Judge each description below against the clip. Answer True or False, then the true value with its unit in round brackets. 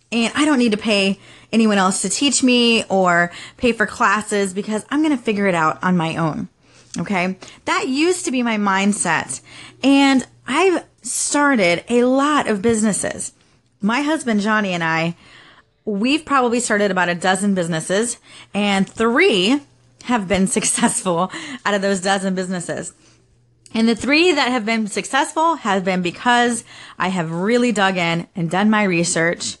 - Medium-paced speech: True (160 wpm)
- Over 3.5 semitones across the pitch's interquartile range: True (4.7 semitones)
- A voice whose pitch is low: False (210 Hz)